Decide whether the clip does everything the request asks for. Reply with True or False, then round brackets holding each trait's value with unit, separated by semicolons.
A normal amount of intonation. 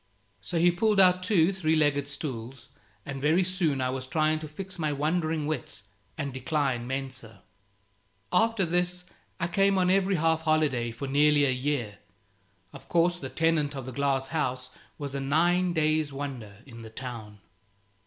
True (4.6 semitones)